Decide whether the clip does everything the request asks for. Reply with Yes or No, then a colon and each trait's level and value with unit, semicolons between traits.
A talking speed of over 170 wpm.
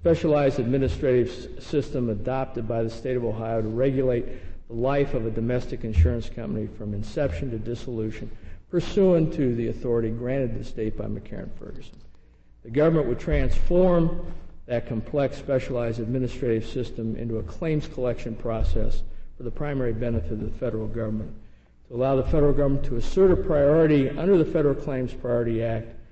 No: average, 160 wpm